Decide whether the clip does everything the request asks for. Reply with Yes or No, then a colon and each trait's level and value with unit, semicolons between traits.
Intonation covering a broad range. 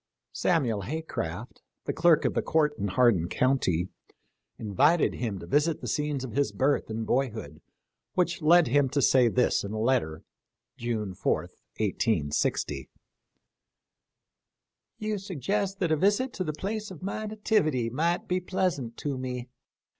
Yes: wide, 7.2 semitones